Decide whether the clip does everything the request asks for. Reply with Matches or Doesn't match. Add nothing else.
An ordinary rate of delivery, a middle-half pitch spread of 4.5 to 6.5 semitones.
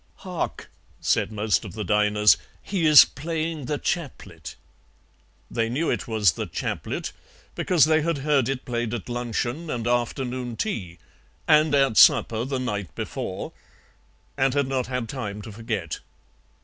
Matches